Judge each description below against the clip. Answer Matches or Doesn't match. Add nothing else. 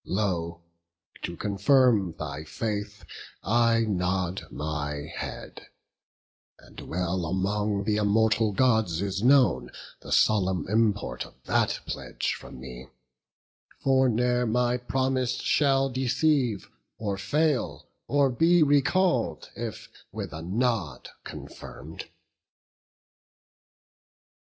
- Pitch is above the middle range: Doesn't match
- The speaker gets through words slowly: Matches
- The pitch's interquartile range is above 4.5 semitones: Matches